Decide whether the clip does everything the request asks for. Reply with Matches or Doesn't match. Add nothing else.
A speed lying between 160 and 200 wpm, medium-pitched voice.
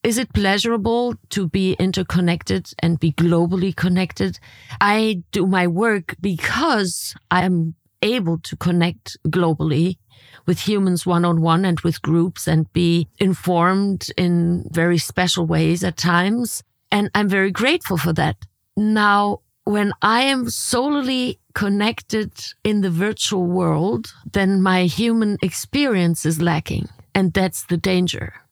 Doesn't match